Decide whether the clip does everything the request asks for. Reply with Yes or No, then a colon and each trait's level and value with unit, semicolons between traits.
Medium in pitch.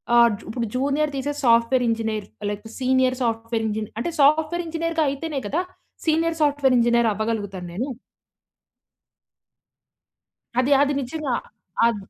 No: very high, 255 Hz